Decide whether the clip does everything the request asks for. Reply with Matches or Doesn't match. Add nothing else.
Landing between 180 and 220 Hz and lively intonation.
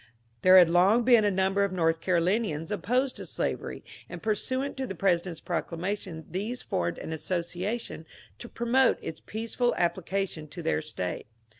Doesn't match